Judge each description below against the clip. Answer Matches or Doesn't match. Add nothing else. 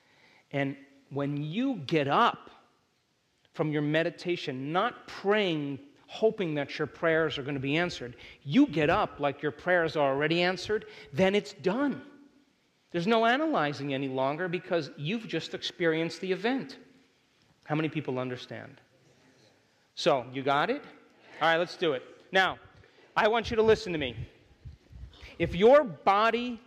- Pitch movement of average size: Doesn't match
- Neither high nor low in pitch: Matches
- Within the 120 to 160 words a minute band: Matches